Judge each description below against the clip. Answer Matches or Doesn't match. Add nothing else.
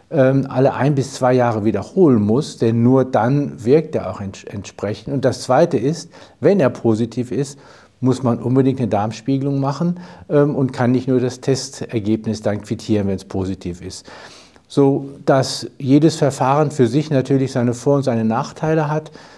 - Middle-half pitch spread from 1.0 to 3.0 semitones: Doesn't match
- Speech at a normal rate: Matches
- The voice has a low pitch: Matches